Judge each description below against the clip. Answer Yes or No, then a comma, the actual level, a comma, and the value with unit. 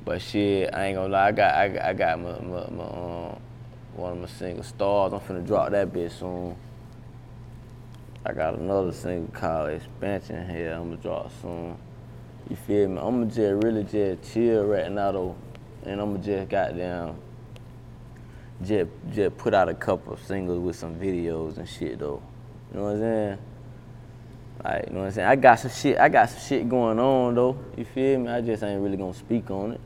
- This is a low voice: Yes, low, 105 Hz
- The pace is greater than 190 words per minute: Yes, average, 200 wpm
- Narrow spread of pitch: No, average, 4.7 semitones